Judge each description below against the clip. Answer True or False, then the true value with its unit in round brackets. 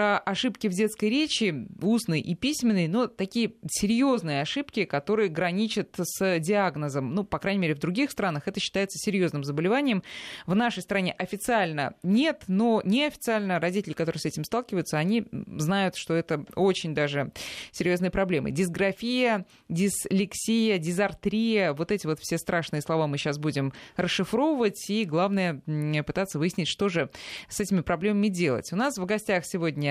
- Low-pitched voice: False (190 Hz)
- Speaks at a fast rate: False (150 wpm)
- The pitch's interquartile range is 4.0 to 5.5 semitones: True (4.3 semitones)